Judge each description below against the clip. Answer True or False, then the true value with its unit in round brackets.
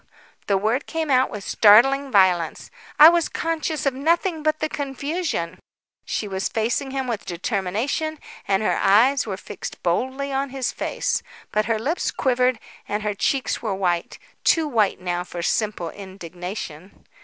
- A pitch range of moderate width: False (6.3 semitones)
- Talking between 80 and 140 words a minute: False (155 wpm)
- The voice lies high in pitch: True (230 Hz)